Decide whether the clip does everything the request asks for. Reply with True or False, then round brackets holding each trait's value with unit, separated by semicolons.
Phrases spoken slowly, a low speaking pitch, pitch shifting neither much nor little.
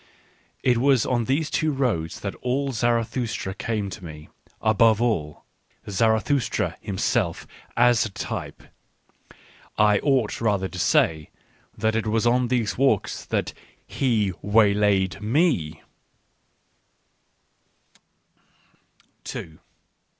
True (105 wpm; 110 Hz; 3.7 semitones)